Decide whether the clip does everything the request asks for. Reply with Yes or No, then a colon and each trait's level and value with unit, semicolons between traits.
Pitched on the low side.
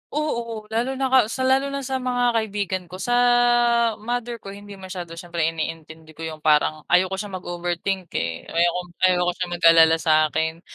No: medium, 185 Hz